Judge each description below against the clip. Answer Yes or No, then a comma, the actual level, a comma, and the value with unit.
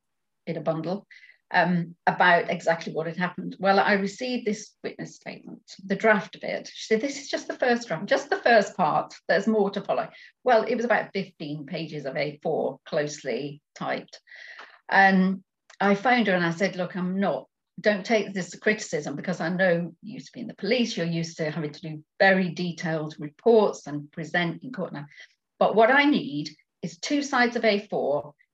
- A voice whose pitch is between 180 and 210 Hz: Yes, high, 190 Hz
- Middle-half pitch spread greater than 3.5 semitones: Yes, average, 4.8 semitones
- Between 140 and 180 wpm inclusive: No, average, 195 wpm